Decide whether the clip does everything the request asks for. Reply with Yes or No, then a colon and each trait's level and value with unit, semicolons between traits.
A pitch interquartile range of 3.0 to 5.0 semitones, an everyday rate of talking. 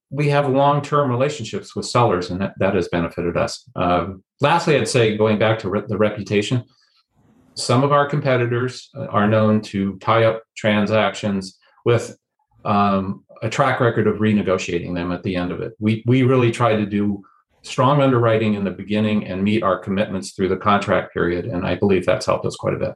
Yes: average, 4.1 semitones; average, 195 wpm